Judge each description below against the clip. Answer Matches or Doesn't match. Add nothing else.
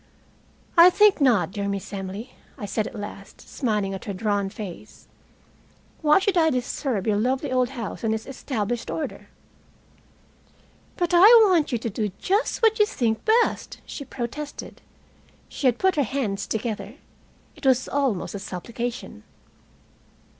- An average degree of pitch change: Doesn't match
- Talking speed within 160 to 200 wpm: Doesn't match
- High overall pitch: Matches